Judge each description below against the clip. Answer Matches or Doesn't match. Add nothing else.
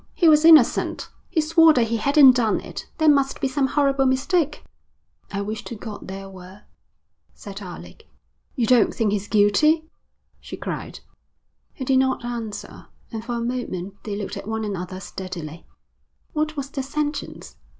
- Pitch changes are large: Matches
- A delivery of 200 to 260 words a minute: Doesn't match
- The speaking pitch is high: Matches